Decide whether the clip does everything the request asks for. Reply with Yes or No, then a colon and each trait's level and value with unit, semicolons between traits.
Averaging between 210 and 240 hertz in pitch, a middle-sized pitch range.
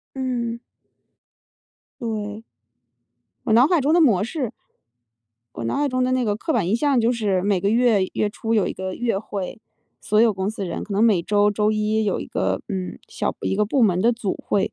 Yes: high, 215 Hz; average, 3.1 semitones